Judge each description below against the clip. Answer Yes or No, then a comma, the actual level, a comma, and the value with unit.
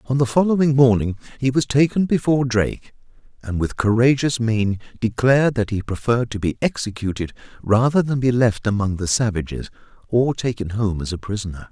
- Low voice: Yes, low, 115 Hz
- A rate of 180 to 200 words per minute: No, average, 170 wpm